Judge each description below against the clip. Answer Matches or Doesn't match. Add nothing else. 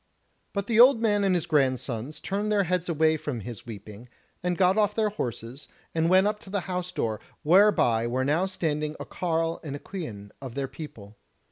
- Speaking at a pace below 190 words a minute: Doesn't match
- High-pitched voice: Doesn't match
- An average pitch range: Doesn't match